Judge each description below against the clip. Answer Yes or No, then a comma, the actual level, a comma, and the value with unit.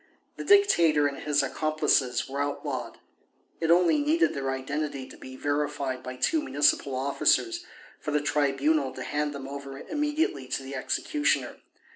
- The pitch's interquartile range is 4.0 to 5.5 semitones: No, average, 2.9 semitones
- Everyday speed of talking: Yes, average, 150 wpm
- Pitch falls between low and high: Yes, medium, 145 Hz